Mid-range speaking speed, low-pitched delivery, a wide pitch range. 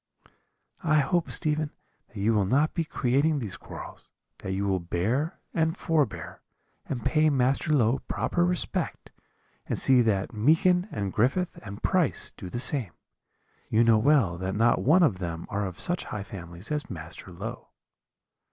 Yes: average, 160 wpm; low, 120 Hz; wide, 7.6 semitones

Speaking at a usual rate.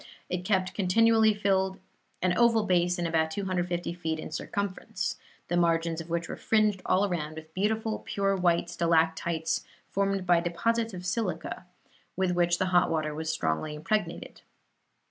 Yes: average, 150 wpm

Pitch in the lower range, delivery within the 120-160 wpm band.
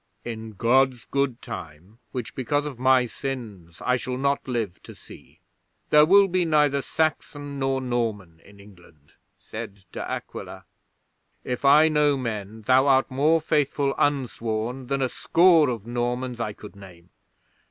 Yes: low, 125 Hz; average, 150 wpm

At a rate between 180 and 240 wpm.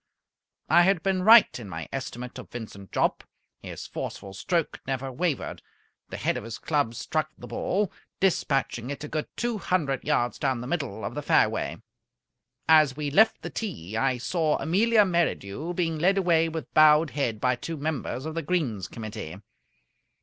No: average, 170 wpm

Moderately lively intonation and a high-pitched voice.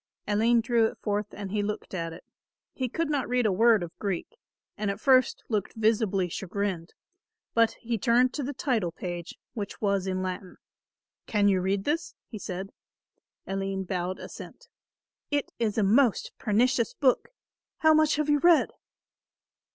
Yes: average, 4.4 semitones; high, 210 Hz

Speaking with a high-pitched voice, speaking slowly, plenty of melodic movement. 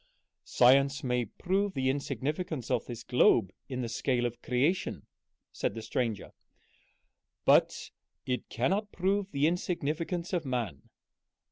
No: low, 135 Hz; slow, 125 wpm; wide, 5.9 semitones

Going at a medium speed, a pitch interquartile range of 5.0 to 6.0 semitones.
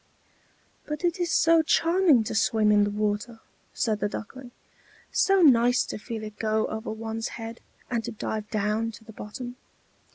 No: average, 170 wpm; average, 3.1 semitones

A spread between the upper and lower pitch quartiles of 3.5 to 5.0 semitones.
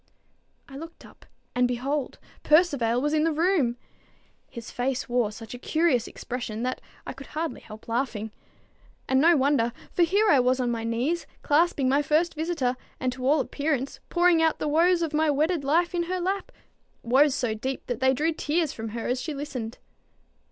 Yes: average, 4.7 semitones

